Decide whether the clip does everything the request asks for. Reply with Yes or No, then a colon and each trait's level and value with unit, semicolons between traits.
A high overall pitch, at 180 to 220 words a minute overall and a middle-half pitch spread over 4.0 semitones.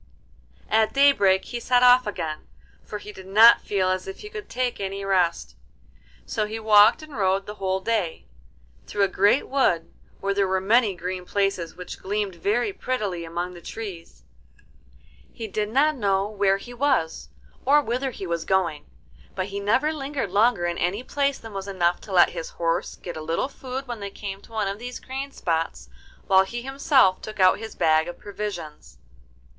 Yes: high, 200 Hz; average, 185 wpm; average, 4.5 semitones